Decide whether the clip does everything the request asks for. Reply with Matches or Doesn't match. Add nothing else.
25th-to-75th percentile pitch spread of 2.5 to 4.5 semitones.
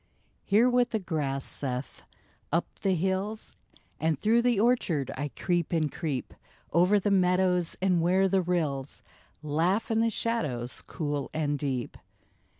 Doesn't match